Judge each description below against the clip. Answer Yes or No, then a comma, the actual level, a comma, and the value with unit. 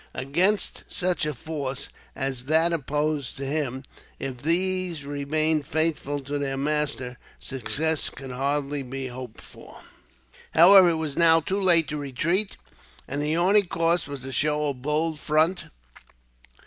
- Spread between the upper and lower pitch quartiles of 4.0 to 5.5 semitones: No, average, 3.2 semitones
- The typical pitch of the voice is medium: Yes, medium, 150 Hz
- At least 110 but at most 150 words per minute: Yes, average, 145 wpm